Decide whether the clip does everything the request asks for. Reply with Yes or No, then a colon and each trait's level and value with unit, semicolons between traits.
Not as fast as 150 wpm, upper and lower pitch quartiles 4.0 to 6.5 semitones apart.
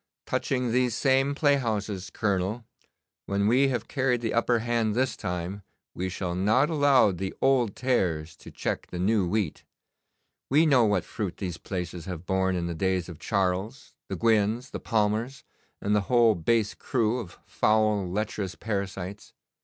No: average, 160 wpm; average, 4.4 semitones